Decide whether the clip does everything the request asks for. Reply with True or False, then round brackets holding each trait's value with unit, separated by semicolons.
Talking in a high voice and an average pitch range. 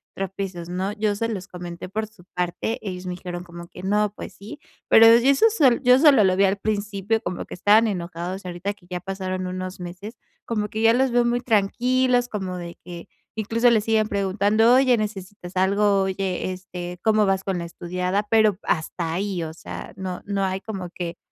True (195 Hz; 3.2 semitones)